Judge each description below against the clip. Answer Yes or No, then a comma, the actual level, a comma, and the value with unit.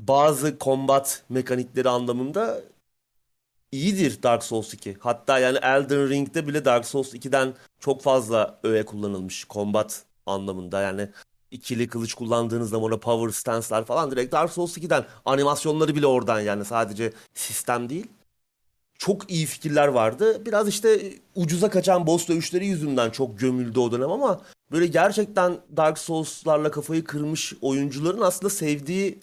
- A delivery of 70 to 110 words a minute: No, fast, 140 wpm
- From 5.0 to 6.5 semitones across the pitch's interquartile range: Yes, wide, 5.4 semitones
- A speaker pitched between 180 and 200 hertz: No, low, 135 Hz